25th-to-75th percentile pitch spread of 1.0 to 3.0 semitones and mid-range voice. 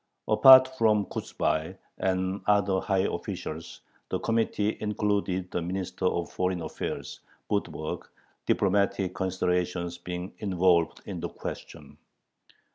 No: narrow, 2.4 semitones; very low, 95 Hz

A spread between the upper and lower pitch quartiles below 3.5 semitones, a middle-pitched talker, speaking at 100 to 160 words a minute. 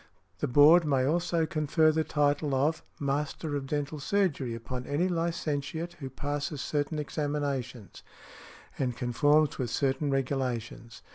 Yes: average, 2.7 semitones; medium, 145 Hz; slow, 135 wpm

